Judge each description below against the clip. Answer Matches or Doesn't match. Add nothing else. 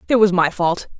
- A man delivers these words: Doesn't match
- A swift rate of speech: Matches